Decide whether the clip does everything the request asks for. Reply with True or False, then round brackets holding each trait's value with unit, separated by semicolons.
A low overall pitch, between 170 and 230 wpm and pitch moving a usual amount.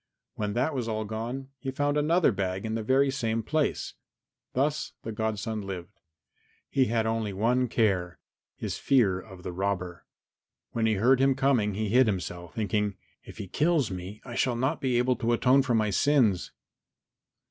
True (115 Hz; 175 wpm; 4.5 semitones)